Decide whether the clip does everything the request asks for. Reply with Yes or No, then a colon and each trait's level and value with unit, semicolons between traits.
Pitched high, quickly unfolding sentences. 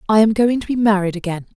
Yes: high, 210 Hz; fast, 265 wpm